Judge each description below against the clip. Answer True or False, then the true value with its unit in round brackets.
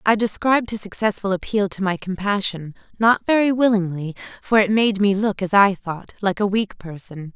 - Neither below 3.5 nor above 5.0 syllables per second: False (5.2 syllables/s)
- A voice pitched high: True (200 Hz)